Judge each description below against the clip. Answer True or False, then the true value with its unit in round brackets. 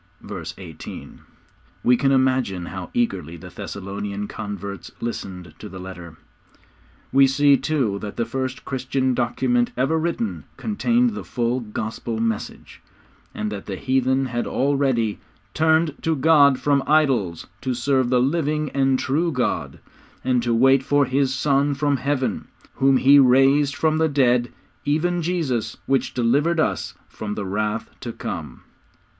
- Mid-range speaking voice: False (130 Hz)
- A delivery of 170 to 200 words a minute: False (150 wpm)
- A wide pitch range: False (4.6 semitones)